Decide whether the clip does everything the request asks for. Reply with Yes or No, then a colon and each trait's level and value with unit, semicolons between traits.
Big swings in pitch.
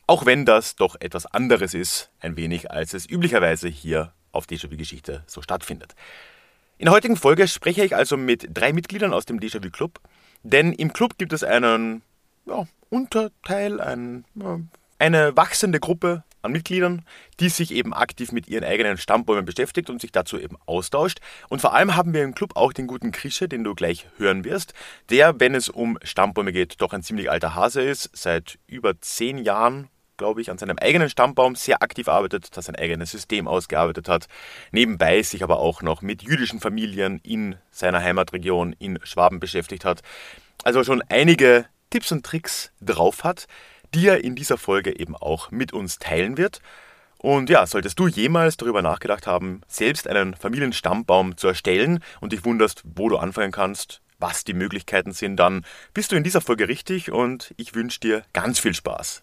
Yes: wide, 8.7 semitones